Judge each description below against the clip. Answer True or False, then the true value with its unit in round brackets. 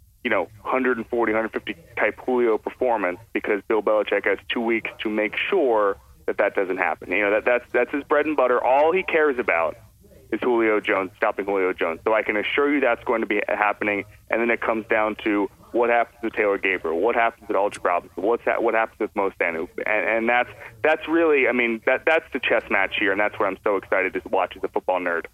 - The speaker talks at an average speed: False (225 wpm)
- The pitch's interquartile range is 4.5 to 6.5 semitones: False (2.7 semitones)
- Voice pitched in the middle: False (115 Hz)